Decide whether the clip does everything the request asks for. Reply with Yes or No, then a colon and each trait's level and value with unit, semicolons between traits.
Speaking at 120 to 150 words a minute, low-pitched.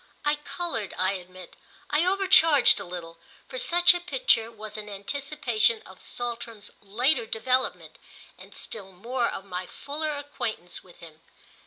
No: average, 145 wpm; high, 230 Hz